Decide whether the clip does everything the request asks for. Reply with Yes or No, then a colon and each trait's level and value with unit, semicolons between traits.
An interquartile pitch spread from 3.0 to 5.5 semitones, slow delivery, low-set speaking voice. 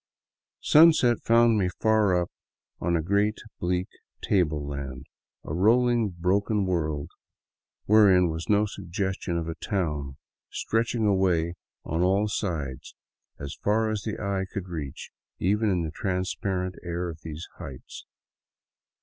Yes: average, 4.1 semitones; slow, 130 wpm; very low, 90 Hz